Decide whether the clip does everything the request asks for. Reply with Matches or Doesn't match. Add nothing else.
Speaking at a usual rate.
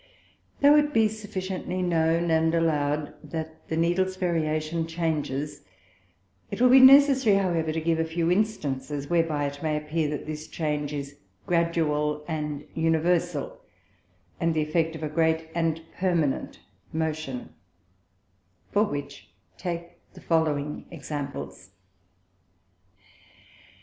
Doesn't match